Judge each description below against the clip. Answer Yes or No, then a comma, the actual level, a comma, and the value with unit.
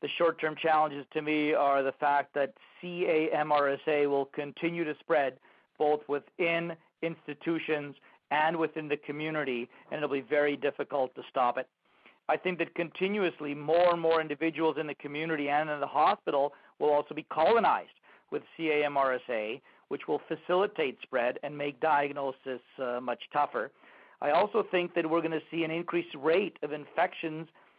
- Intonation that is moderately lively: No, narrow, 2.2 semitones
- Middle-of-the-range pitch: Yes, medium, 150 Hz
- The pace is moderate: Yes, average, 160 wpm